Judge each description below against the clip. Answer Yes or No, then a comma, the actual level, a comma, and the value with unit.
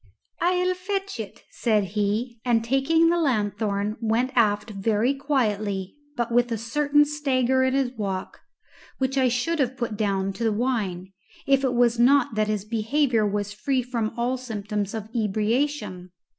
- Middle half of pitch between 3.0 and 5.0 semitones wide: Yes, average, 4.1 semitones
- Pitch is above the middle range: Yes, high, 235 Hz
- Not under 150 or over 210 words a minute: Yes, average, 160 wpm